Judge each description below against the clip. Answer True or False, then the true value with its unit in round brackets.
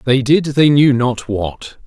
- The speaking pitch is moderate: False (130 Hz)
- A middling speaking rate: True (195 wpm)